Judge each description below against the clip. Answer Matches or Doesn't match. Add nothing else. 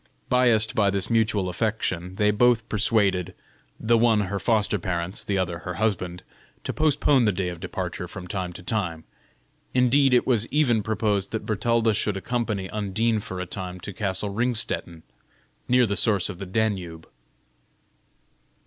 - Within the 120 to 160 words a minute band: Matches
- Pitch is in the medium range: Doesn't match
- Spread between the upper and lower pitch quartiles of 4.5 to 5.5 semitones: Doesn't match